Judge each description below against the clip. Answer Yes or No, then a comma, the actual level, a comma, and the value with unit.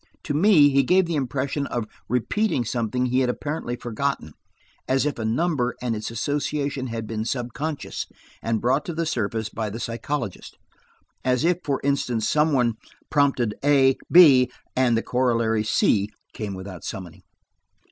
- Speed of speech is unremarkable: Yes, average, 155 wpm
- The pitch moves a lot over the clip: No, average, 4.1 semitones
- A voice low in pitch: Yes, low, 125 Hz